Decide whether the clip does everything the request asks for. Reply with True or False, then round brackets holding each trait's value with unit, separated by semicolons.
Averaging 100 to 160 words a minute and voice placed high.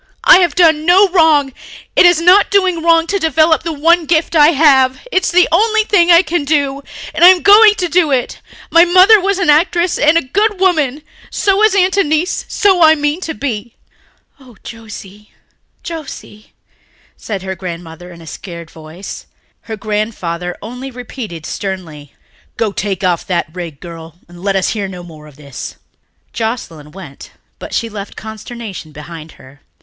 False (175 wpm; 270 Hz)